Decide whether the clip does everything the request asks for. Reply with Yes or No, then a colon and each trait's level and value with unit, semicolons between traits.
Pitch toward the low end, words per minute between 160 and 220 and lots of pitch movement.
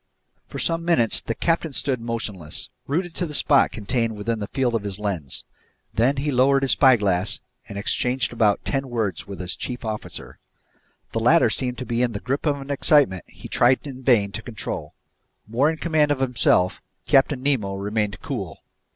No: low, 125 Hz; average, 185 wpm; average, 4.7 semitones